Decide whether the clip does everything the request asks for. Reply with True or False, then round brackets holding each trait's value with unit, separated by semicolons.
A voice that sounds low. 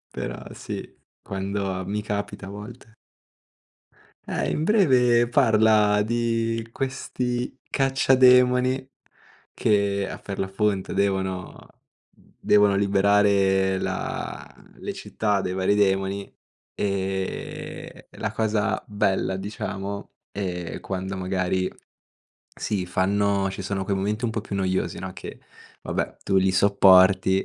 True (100 Hz)